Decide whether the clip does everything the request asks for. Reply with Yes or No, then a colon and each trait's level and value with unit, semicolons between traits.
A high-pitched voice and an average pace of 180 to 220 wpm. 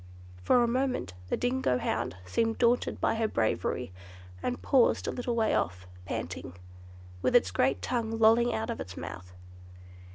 No: high, 225 Hz; average, 160 wpm